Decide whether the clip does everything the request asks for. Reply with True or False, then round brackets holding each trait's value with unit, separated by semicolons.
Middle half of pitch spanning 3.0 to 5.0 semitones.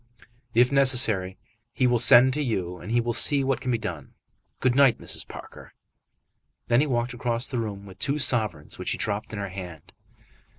True (4.2 semitones)